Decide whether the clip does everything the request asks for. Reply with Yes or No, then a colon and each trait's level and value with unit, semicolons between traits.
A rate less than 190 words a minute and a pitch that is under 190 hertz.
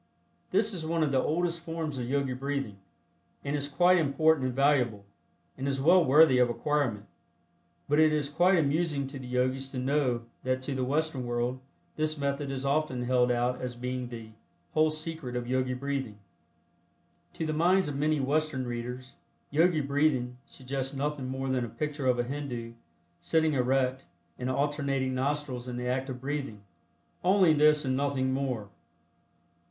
Yes: average, 170 wpm; low, 135 Hz